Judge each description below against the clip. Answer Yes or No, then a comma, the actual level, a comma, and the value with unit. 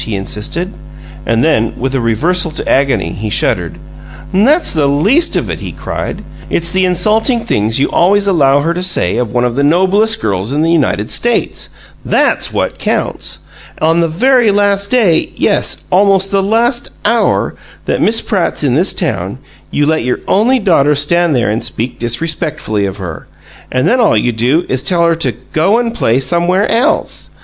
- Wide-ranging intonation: Yes, wide, 8.0 semitones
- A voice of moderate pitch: Yes, medium, 165 Hz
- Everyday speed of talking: Yes, average, 180 wpm